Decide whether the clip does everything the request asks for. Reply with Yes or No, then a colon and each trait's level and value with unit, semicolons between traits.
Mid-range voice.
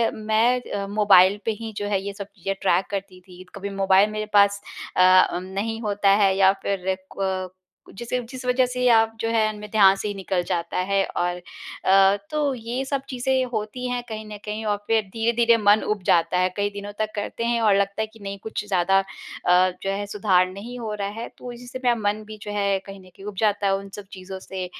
No: high, 205 Hz